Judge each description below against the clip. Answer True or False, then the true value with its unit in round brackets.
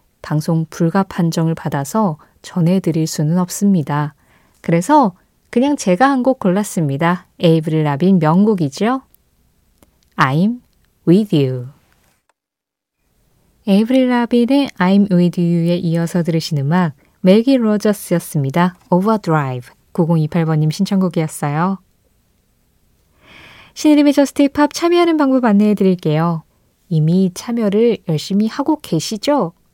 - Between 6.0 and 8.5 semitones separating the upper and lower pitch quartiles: False (5.1 semitones)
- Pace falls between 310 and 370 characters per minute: False (280 characters per minute)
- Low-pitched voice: False (180 Hz)